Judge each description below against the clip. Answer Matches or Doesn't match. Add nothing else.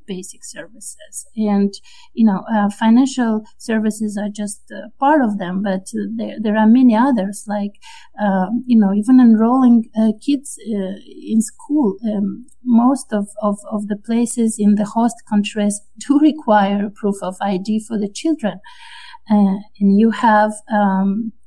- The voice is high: Matches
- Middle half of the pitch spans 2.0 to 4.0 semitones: Matches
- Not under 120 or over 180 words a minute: Matches